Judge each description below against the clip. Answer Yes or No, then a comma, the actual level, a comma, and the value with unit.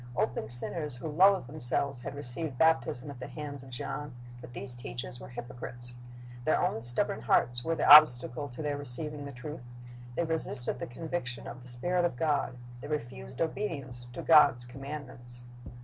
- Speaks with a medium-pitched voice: No, low, 130 Hz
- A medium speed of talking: Yes, average, 170 wpm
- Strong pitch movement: No, average, 3.7 semitones